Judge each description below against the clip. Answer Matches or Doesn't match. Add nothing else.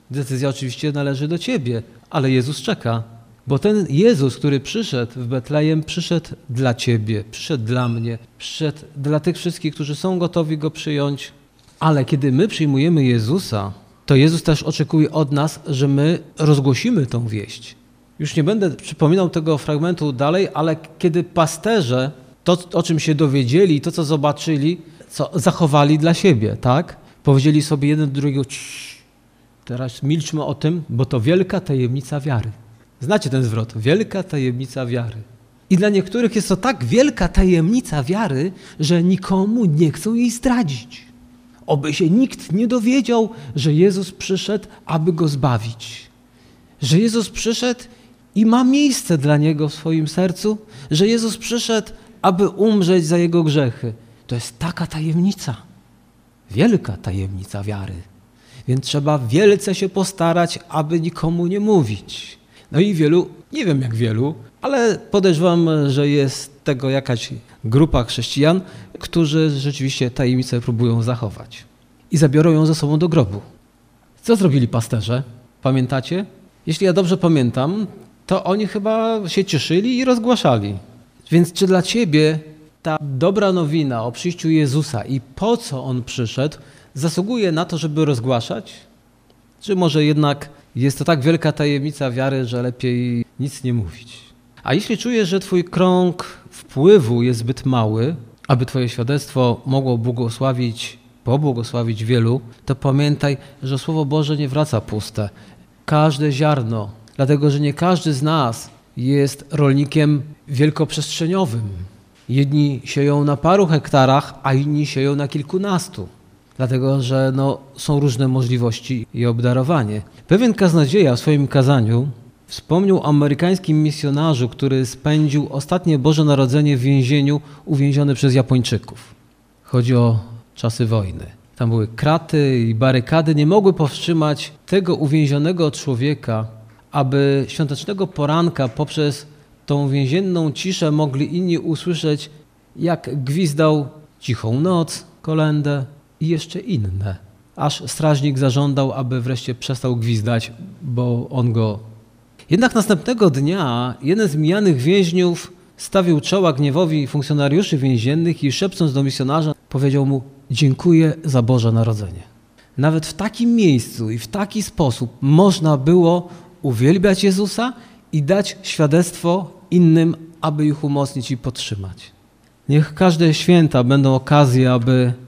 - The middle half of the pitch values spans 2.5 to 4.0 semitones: Doesn't match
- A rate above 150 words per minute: Doesn't match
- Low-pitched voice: Doesn't match